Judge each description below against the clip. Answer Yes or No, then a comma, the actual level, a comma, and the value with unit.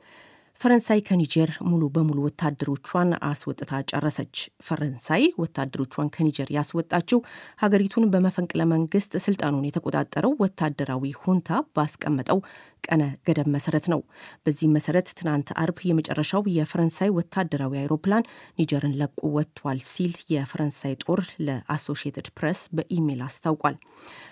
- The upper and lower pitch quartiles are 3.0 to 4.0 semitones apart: Yes, average, 3.4 semitones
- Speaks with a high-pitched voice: No, medium, 155 Hz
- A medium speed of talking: Yes, average, 100 wpm